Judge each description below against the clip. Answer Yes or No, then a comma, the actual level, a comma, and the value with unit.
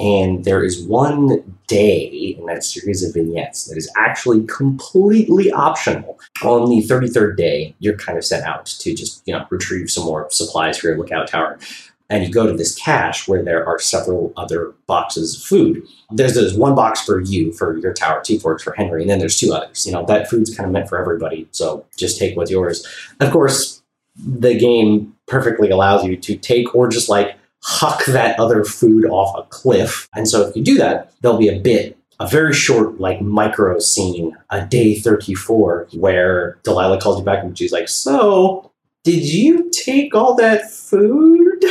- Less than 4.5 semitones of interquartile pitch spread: No, wide, 5.4 semitones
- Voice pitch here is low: Yes, low, 105 Hz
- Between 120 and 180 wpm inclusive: No, average, 195 wpm